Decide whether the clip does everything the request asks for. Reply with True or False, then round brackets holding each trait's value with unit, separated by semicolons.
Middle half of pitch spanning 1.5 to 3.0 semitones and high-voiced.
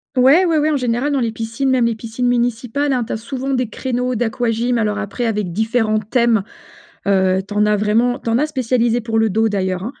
True (2.6 semitones; 235 Hz)